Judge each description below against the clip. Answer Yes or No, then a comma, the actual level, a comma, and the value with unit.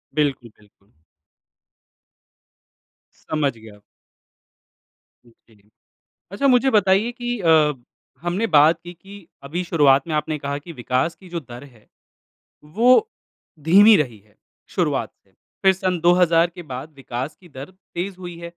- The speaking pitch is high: No, medium, 165 Hz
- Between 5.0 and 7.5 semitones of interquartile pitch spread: Yes, wide, 5.5 semitones